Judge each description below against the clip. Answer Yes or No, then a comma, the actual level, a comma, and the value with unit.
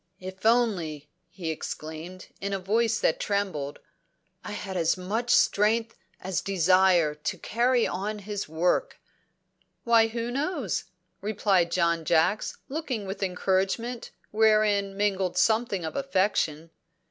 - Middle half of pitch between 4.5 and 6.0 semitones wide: No, average, 3.9 semitones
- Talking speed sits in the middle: No, slow, 125 wpm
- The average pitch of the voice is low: No, high, 195 Hz